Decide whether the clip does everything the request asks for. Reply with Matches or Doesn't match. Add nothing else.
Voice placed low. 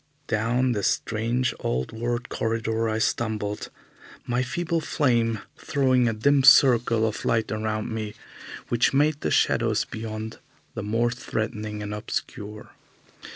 Matches